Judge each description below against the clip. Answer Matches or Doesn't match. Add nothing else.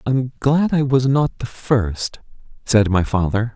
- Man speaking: Matches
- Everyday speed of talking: Matches